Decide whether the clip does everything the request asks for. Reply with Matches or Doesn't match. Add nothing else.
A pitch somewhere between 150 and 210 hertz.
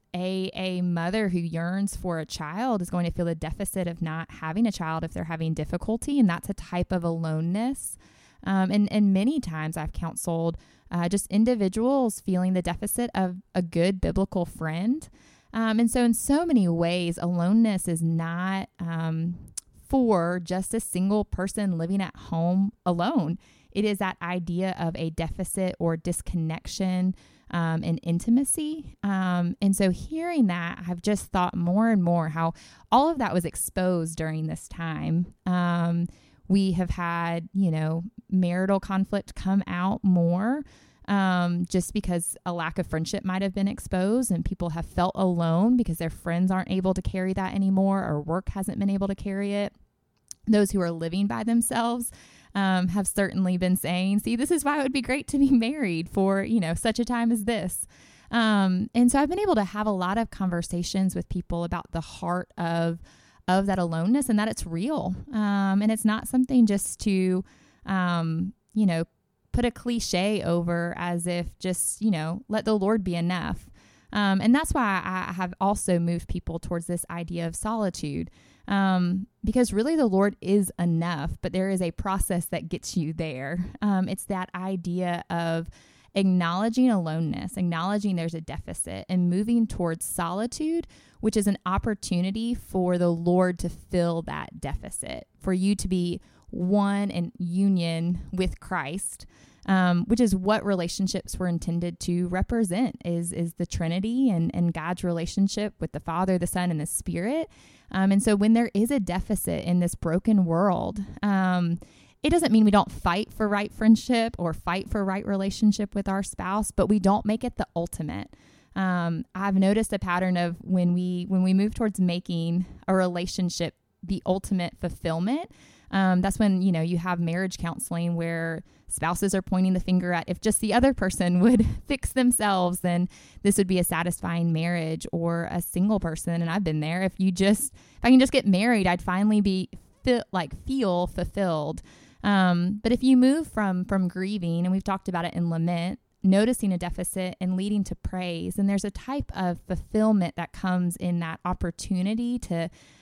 Matches